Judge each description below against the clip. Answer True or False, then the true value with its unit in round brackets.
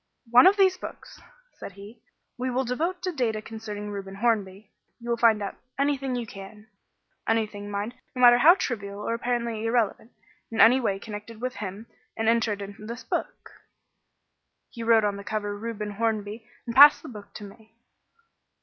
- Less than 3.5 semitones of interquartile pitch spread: True (2.8 semitones)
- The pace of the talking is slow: False (175 wpm)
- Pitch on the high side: True (225 Hz)